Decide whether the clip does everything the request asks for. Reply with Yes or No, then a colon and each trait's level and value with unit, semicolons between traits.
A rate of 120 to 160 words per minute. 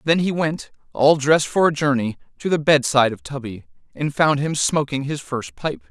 No: fast, 205 wpm